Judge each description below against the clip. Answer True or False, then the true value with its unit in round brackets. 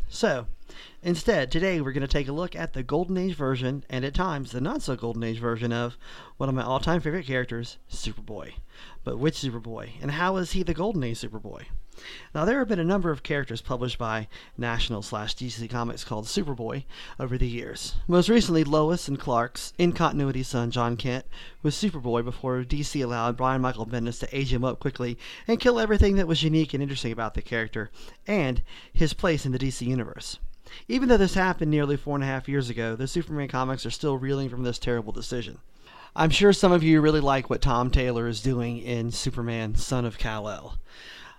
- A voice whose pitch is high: False (130 Hz)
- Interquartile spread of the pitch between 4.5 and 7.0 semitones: True (4.8 semitones)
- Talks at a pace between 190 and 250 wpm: True (205 wpm)